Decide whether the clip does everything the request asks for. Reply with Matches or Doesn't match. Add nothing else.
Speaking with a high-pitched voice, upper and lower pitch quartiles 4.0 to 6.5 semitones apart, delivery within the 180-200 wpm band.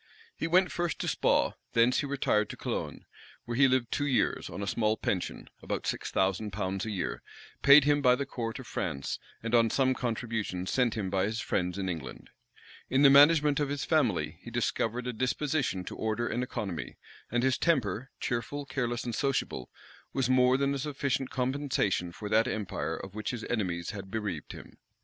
Doesn't match